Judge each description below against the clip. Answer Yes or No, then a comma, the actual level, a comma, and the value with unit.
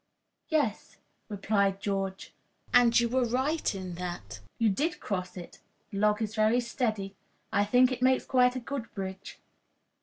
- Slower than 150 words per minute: No, average, 155 wpm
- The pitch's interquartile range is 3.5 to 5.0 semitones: Yes, average, 4.1 semitones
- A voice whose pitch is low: No, high, 215 Hz